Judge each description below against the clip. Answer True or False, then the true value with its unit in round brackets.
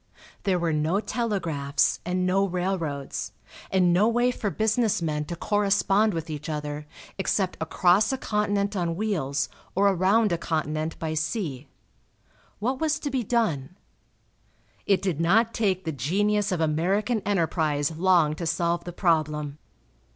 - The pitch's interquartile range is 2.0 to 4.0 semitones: False (4.7 semitones)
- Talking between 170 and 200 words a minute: False (145 wpm)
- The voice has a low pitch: False (180 Hz)